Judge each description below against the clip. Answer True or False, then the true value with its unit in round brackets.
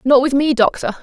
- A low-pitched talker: False (265 Hz)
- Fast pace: True (235 wpm)